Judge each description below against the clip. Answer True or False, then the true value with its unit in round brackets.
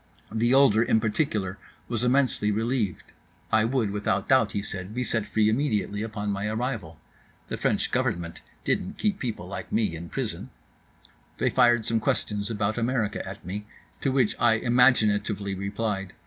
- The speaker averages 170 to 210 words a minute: False (150 wpm)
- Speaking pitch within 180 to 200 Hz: False (110 Hz)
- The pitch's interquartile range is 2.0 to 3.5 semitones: True (2.9 semitones)